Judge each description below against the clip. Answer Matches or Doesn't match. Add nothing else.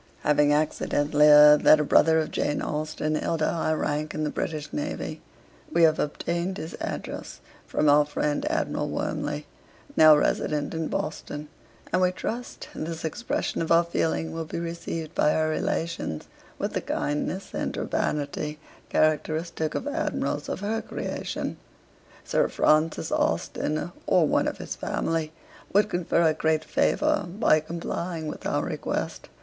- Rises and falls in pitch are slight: Matches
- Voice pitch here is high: Doesn't match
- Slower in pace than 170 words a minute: Matches